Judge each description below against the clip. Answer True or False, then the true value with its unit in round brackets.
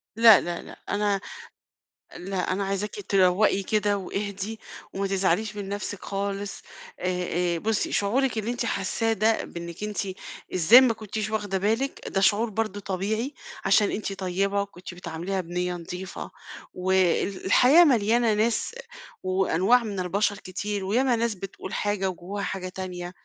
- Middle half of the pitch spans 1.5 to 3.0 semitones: True (2.5 semitones)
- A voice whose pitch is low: False (200 Hz)